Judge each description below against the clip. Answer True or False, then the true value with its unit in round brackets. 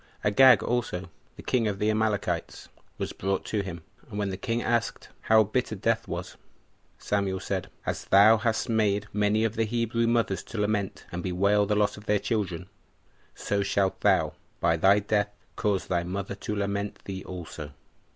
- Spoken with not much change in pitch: True (2.3 semitones)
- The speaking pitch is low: True (105 Hz)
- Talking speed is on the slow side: False (175 wpm)